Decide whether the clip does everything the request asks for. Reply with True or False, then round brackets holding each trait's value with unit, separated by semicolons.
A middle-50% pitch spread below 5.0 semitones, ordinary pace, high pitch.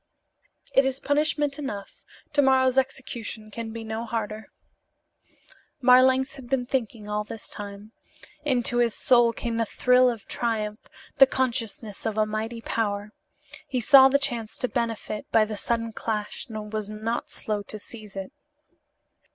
True (3.2 semitones; 155 wpm; 230 Hz)